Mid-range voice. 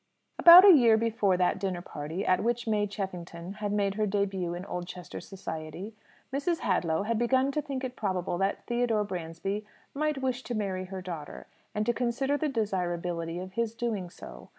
No: high, 200 Hz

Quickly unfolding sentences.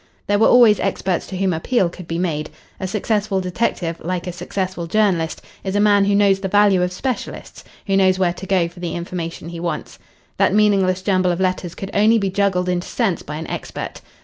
Yes: fast, 210 wpm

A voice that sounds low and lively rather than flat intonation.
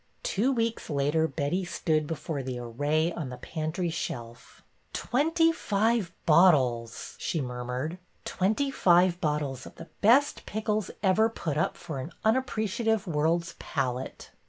No: medium, 165 Hz; wide, 7.0 semitones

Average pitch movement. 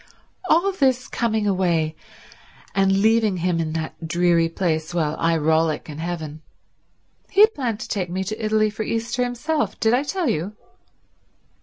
No: wide, 5.8 semitones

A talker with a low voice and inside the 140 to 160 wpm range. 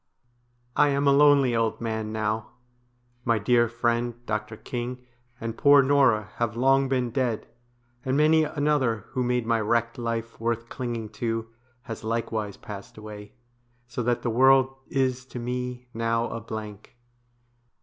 Yes: low, 120 Hz; average, 150 wpm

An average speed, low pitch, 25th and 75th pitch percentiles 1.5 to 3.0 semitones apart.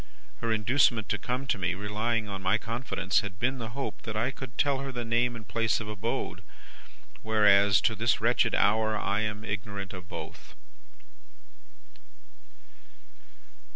Yes: average, 155 wpm; low, 110 Hz; narrow, 2.5 semitones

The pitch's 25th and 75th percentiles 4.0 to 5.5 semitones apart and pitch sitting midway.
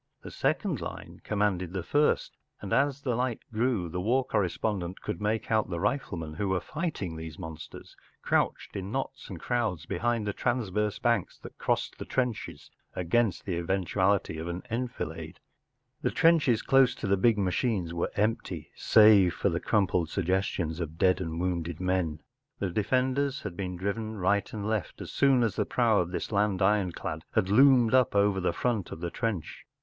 No: average, 4.6 semitones; low, 100 Hz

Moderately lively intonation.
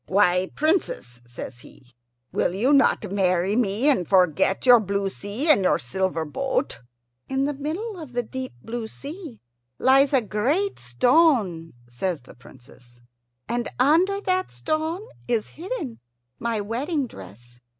No: wide, 8.1 semitones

